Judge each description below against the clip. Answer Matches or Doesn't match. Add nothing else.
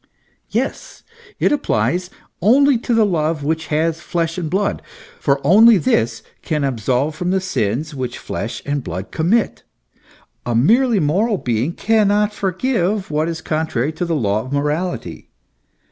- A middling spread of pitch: Doesn't match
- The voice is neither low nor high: Matches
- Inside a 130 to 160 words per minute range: Matches